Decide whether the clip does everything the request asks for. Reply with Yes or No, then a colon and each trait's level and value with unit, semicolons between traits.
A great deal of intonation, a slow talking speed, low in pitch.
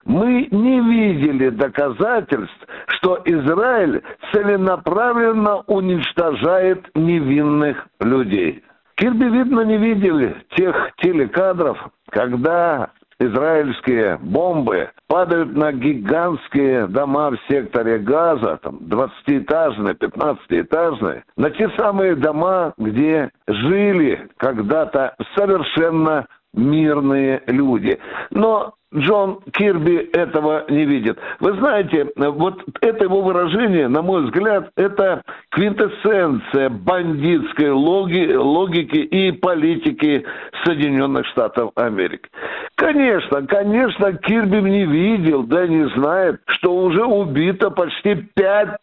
No: wide, 5.8 semitones; slow, 95 wpm; medium, 180 Hz